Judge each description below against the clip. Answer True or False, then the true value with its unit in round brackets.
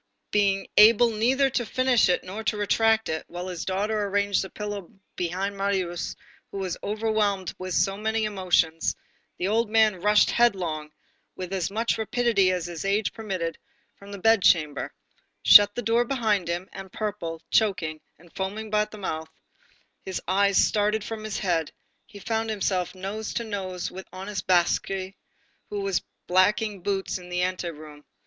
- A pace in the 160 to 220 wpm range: True (165 wpm)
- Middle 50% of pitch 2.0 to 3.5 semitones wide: True (2.9 semitones)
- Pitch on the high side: True (200 Hz)